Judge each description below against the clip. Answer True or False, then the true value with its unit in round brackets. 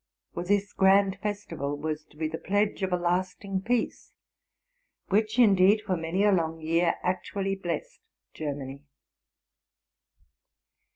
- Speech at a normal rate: False (125 wpm)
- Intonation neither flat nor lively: True (3.8 semitones)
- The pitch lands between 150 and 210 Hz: True (185 Hz)